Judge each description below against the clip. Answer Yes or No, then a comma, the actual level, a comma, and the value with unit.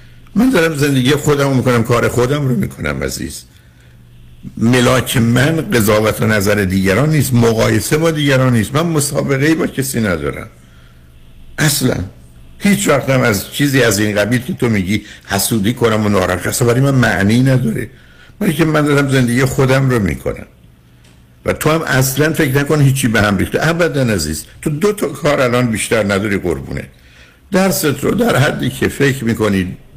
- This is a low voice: Yes, low, 120 Hz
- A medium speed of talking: No, fast, 170 wpm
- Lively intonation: Yes, wide, 6.3 semitones